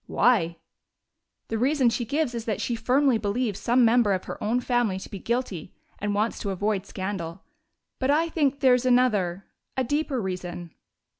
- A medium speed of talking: Yes, average, 170 wpm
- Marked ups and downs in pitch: No, average, 4.4 semitones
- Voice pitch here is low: No, high, 230 Hz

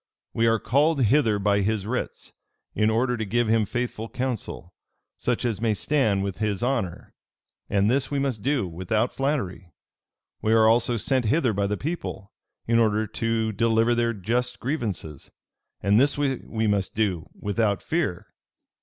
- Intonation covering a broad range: No, average, 3.4 semitones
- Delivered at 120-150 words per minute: No, average, 160 wpm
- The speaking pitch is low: Yes, low, 110 Hz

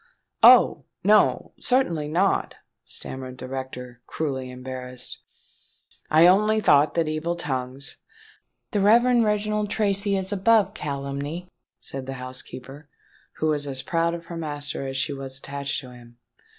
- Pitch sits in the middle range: Yes, medium, 145 Hz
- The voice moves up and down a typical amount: No, wide, 6.1 semitones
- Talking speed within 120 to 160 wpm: Yes, slow, 135 wpm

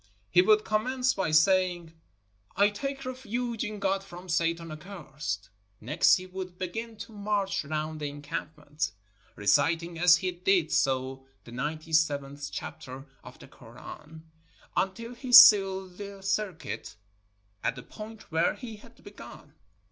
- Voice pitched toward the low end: No, medium, 180 Hz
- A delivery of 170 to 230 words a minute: No, average, 140 wpm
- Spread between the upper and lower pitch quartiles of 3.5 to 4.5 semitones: No, average, 5.0 semitones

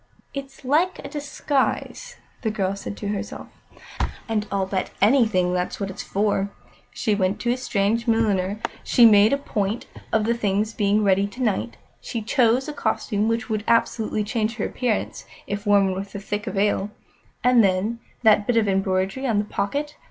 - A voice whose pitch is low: No, high, 210 Hz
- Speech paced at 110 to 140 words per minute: No, average, 175 wpm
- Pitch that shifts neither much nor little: Yes, average, 3.0 semitones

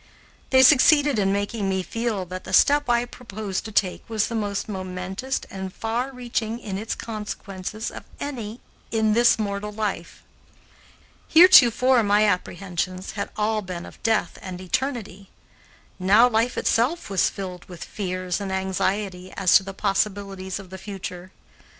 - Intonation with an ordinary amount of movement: Yes, average, 3.3 semitones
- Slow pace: No, average, 150 wpm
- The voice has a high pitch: Yes, high, 205 Hz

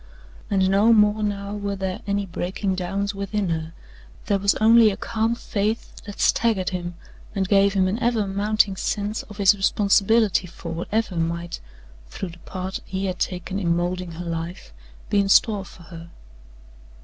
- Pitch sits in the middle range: No, high, 195 Hz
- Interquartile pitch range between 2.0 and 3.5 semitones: Yes, narrow, 2.4 semitones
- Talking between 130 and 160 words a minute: No, average, 170 wpm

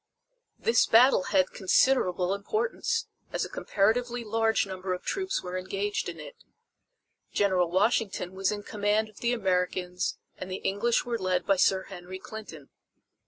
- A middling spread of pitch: Yes, average, 3.5 semitones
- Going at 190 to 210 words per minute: No, average, 150 wpm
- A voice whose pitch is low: No, high, 200 Hz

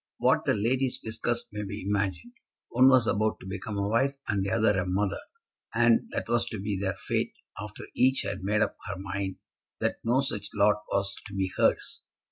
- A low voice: Yes, low, 105 Hz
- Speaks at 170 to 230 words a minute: Yes, average, 200 wpm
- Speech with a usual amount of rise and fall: Yes, average, 3.0 semitones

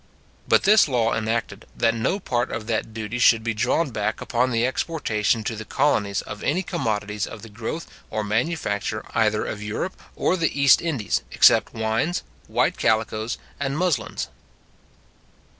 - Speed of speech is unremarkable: Yes, average, 160 wpm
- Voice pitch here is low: Yes, low, 115 Hz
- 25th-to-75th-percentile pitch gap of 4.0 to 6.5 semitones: Yes, average, 4.4 semitones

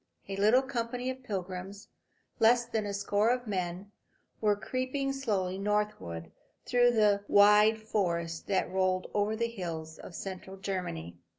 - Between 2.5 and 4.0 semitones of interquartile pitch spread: Yes, average, 3.7 semitones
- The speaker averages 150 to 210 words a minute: No, average, 140 wpm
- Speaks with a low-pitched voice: No, high, 205 Hz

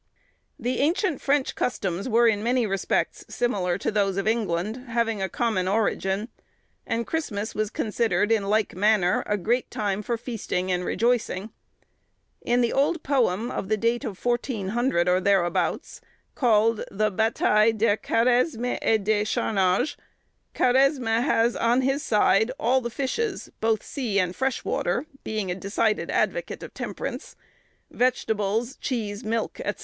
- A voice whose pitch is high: Yes, high, 225 Hz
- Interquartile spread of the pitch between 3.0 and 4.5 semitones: Yes, average, 3.3 semitones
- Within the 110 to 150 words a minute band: Yes, average, 145 wpm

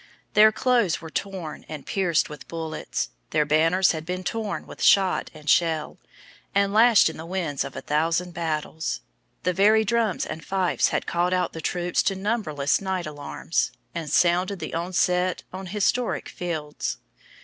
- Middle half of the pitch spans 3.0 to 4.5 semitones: Yes, average, 3.4 semitones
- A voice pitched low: No, medium, 175 Hz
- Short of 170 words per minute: Yes, average, 160 wpm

